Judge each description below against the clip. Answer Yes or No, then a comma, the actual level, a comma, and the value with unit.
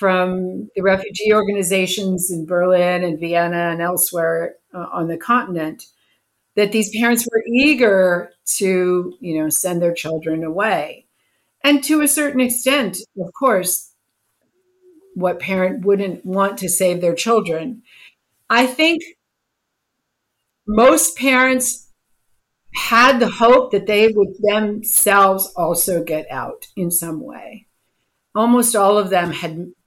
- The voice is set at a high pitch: Yes, high, 195 Hz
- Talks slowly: Yes, slow, 125 wpm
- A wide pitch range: No, average, 4.8 semitones